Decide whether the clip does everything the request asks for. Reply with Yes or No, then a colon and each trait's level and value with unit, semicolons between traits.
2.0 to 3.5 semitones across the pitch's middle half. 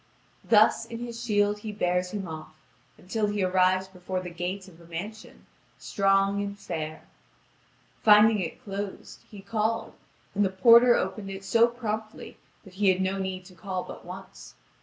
Yes: narrow, 2.5 semitones